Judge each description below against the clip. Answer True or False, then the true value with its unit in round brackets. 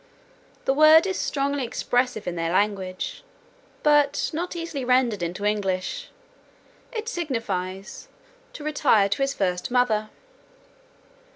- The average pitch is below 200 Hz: False (245 Hz)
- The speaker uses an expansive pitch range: True (7.0 semitones)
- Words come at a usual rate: False (115 wpm)